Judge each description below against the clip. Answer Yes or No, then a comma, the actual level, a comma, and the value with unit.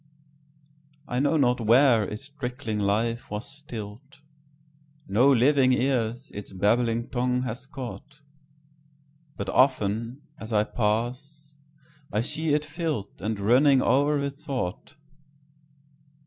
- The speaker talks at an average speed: No, slow, 105 wpm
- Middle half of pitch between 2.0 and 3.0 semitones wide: No, average, 4.3 semitones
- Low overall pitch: Yes, low, 130 Hz